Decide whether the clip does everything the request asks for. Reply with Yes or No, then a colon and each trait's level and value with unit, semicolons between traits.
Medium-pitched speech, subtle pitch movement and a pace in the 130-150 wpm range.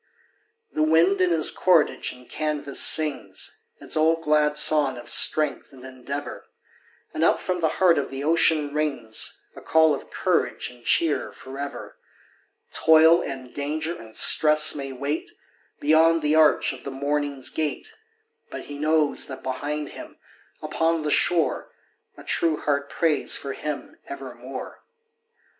Yes: medium, 150 Hz; narrow, 2.2 semitones; average, 145 wpm